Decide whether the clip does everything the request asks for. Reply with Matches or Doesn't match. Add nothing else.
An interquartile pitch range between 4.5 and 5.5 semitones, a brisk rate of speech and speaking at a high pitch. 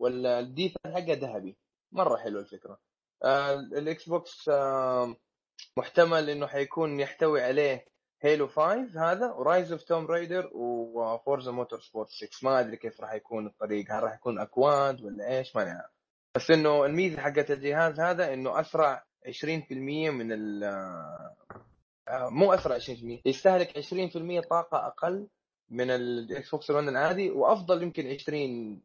Doesn't match